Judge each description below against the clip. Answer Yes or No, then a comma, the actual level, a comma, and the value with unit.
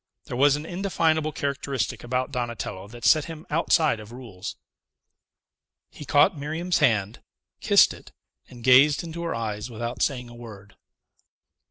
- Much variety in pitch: No, average, 4.7 semitones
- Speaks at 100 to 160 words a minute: Yes, average, 145 wpm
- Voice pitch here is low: Yes, low, 130 Hz